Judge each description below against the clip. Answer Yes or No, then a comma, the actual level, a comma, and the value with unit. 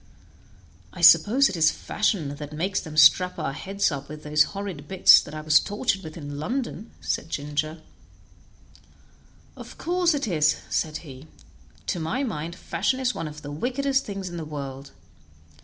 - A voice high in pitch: No, medium, 165 Hz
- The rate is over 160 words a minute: Yes, average, 170 wpm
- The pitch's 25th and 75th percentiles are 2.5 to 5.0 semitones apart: No, wide, 5.5 semitones